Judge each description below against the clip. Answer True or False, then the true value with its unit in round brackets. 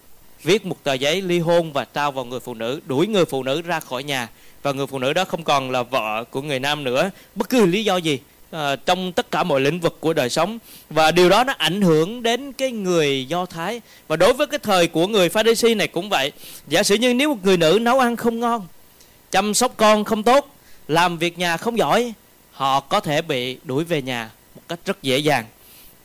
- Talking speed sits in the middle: True (240 wpm)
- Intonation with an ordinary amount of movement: False (7.0 semitones)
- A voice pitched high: False (170 Hz)